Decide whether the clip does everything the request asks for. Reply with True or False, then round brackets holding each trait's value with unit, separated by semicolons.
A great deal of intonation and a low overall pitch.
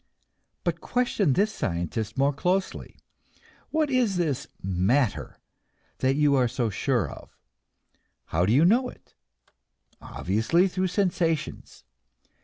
False (8.8 semitones; 145 Hz)